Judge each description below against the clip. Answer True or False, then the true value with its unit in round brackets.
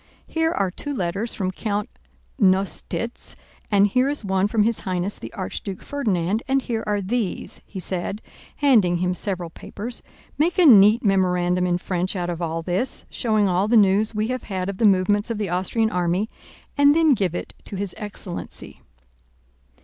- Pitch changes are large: False (3.6 semitones)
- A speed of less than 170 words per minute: False (175 wpm)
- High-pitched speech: True (200 Hz)